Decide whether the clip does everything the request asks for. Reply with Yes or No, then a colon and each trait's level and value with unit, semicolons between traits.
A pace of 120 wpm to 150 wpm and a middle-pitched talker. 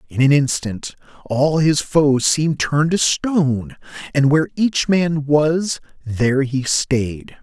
Yes: average, 145 wpm; medium, 145 Hz